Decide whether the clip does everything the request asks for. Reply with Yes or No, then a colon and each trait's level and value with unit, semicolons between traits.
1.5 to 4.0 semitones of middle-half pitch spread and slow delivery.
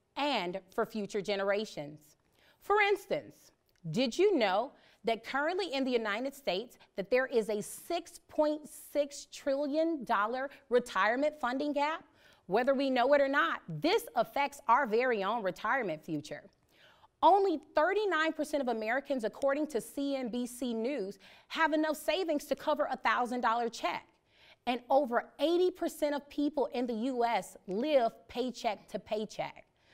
No: average, 4.9 semitones; slow, 130 wpm